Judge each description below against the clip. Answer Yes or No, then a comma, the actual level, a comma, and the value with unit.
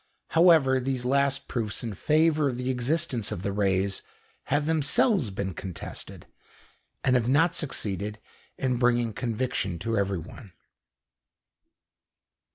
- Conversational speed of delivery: No, slow, 120 wpm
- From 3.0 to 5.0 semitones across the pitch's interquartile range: No, wide, 5.4 semitones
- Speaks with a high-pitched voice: No, low, 125 Hz